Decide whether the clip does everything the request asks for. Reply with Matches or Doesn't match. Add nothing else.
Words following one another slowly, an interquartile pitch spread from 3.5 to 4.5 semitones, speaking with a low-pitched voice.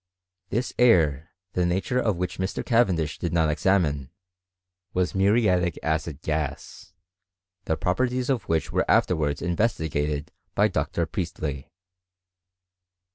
Matches